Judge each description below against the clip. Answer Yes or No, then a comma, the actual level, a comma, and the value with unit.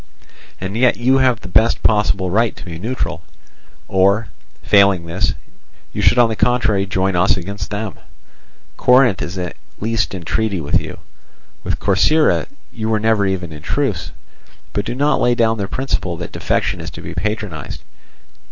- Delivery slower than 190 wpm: Yes, average, 170 wpm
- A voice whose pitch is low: Yes, low, 100 Hz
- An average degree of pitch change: Yes, average, 3.7 semitones